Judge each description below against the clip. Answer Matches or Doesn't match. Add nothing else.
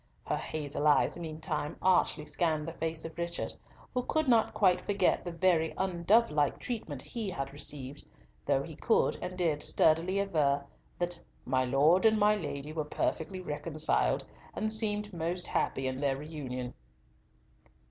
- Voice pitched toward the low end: Doesn't match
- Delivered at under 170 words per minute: Matches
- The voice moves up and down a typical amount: Matches